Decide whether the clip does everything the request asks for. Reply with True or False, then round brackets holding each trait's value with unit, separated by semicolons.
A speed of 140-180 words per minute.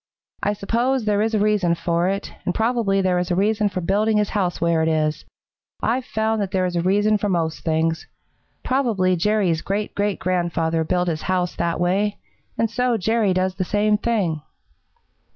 False (190 wpm)